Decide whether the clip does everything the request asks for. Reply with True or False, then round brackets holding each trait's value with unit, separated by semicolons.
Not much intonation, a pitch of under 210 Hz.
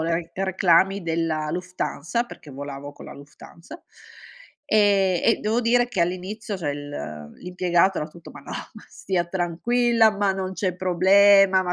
False (3.1 semitones; 185 Hz)